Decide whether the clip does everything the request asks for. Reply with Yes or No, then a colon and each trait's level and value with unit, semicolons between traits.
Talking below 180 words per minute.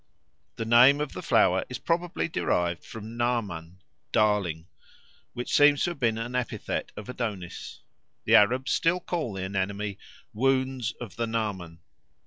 Yes: average, 145 wpm